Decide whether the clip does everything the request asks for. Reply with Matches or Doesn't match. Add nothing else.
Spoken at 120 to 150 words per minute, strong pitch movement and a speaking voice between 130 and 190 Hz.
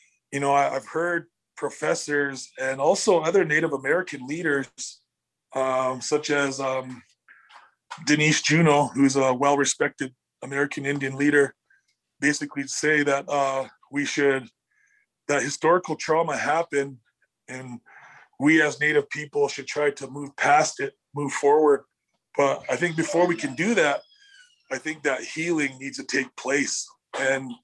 Doesn't match